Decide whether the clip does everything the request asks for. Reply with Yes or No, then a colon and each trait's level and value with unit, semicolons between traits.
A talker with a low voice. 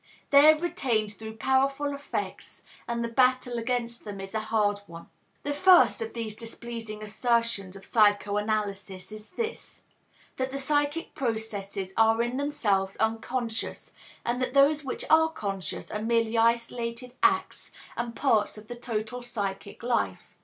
No: high, 230 Hz